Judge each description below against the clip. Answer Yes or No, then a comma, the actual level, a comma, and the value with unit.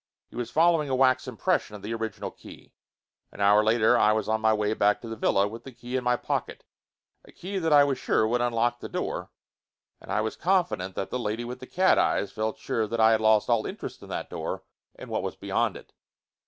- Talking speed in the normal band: No, fast, 235 wpm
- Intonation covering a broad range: No, average, 3.1 semitones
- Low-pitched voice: Yes, low, 115 Hz